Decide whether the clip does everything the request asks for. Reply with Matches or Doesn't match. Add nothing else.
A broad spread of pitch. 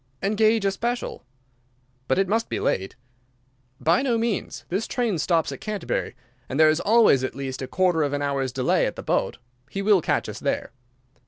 Matches